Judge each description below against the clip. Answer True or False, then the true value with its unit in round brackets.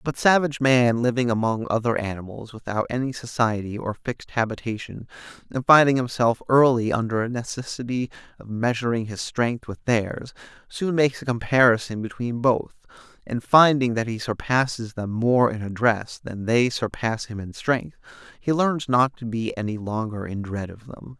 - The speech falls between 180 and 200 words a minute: False (165 wpm)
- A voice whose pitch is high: False (120 Hz)